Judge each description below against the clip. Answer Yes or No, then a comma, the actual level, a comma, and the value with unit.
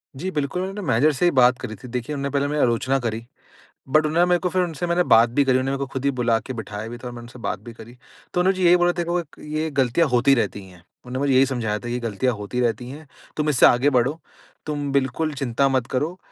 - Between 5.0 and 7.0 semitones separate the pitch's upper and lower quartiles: No, average, 4.3 semitones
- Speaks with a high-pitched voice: No, low, 135 Hz